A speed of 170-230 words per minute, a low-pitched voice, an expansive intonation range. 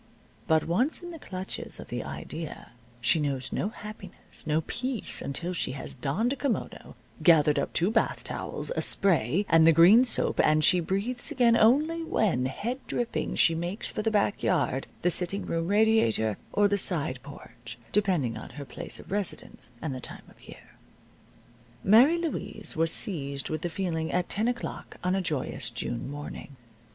No: average, 175 wpm; medium, 175 Hz; wide, 6.9 semitones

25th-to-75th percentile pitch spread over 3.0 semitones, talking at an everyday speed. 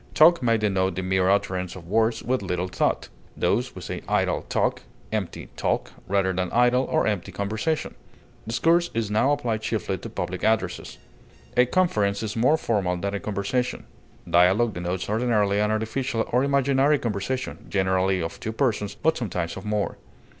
Yes: average, 4.5 semitones; average, 165 wpm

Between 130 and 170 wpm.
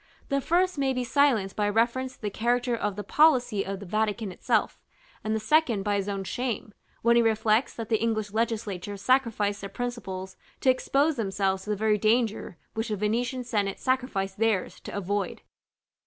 No: average, 185 wpm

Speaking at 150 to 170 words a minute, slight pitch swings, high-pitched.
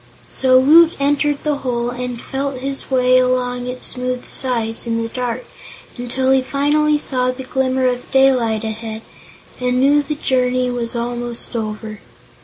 Yes: average, 155 wpm; narrow, 1.8 semitones; very high, 255 Hz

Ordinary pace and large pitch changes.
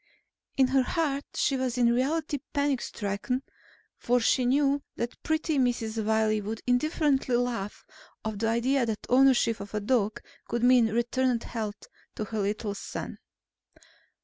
No: average, 145 wpm; average, 3.4 semitones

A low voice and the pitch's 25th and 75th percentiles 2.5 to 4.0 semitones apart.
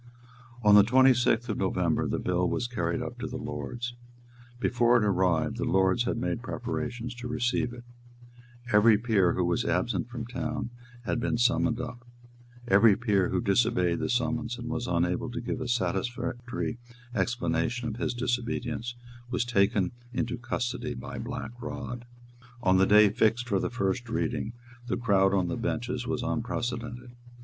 Yes: low, 120 Hz; average, 3.2 semitones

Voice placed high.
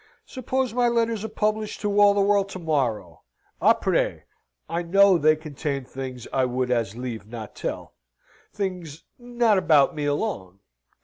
No: medium, 165 Hz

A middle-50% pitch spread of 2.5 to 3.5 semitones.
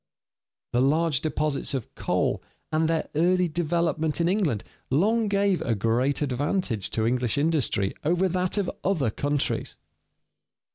No: average, 5.1 semitones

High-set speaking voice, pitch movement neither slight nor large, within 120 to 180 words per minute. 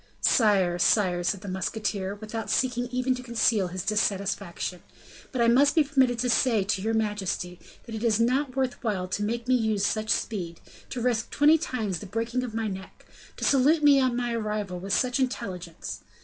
No: high, 220 Hz; average, 4.2 semitones; average, 190 wpm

